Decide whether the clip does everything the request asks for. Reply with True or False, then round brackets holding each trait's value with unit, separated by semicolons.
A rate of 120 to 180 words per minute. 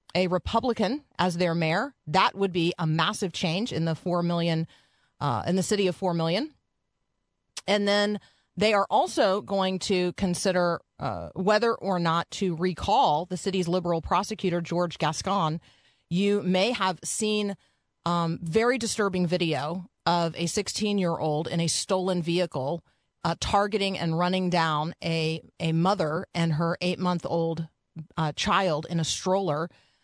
True (145 wpm)